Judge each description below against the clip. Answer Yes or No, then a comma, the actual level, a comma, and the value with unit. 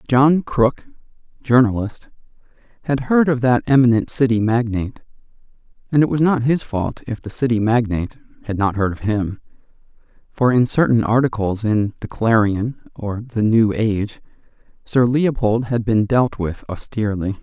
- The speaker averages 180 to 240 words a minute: No, average, 150 wpm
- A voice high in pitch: No, low, 115 Hz